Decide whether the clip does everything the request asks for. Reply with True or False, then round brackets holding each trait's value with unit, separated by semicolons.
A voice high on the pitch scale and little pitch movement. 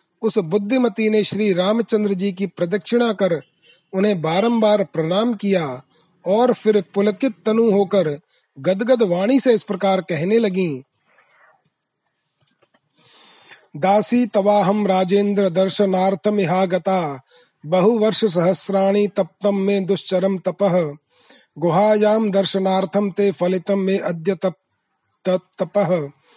True (195 Hz; 2.2 semitones)